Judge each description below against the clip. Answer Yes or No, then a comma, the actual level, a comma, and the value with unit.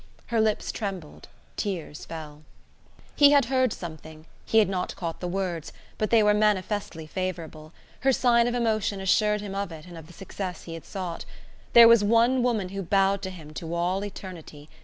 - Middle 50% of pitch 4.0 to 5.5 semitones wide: Yes, average, 4.4 semitones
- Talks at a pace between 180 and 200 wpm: Yes, average, 185 wpm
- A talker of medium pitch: No, high, 195 Hz